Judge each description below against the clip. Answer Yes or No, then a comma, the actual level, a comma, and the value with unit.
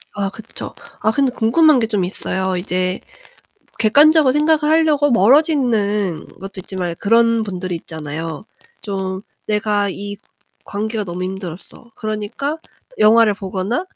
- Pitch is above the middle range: Yes, high, 210 Hz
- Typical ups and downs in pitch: Yes, average, 4.3 semitones